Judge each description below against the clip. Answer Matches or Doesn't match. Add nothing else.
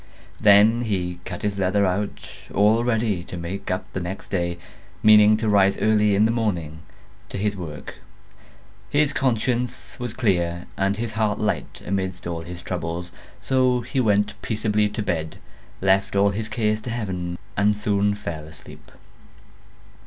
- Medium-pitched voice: Doesn't match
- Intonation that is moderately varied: Matches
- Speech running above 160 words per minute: Doesn't match